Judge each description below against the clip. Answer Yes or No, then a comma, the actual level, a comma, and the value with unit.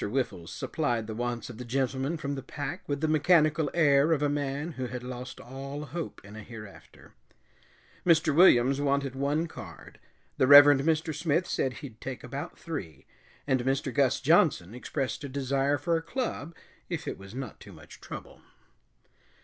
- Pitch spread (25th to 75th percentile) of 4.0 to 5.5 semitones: No, average, 3.3 semitones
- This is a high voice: No, medium, 140 Hz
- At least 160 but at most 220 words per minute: Yes, average, 175 wpm